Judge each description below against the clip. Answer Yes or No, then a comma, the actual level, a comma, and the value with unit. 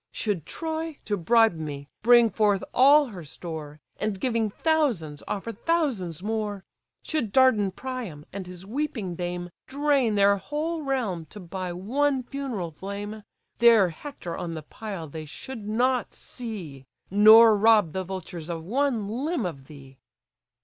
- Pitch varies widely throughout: Yes, wide, 6.4 semitones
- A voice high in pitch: Yes, high, 210 Hz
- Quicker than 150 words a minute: No, average, 145 wpm